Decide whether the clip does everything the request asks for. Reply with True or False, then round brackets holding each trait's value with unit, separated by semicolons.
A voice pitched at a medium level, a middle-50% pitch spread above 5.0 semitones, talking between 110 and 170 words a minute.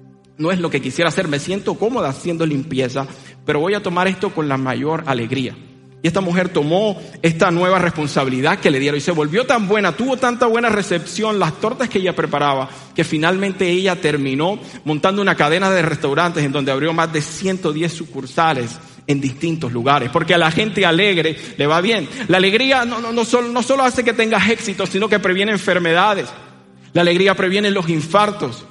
False (170 Hz; 5.5 semitones; 190 wpm)